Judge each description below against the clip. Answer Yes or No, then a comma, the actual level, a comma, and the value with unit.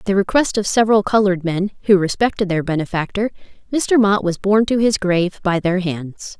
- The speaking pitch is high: Yes, high, 195 Hz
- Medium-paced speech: Yes, average, 195 wpm